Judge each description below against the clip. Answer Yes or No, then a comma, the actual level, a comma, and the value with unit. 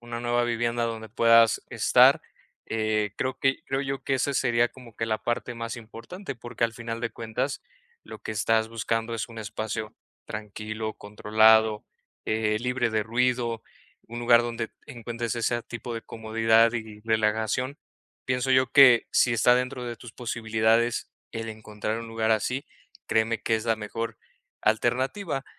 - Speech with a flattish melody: Yes, narrow, 1.5 semitones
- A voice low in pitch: Yes, low, 115 Hz